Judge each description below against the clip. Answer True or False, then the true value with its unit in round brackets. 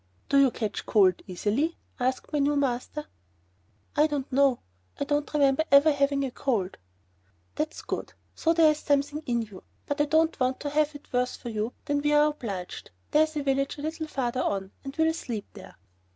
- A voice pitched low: False (280 Hz)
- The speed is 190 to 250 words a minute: True (195 wpm)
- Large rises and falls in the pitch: False (3.4 semitones)